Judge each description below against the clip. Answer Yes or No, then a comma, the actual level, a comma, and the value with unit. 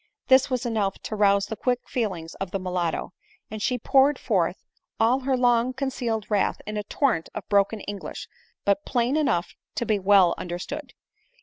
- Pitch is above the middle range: Yes, high, 215 Hz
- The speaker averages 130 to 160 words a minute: No, average, 175 wpm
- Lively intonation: No, average, 4.3 semitones